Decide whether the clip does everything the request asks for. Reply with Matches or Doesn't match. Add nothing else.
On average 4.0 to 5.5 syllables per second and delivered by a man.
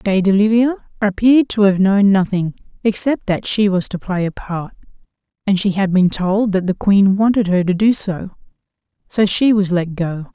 Doesn't match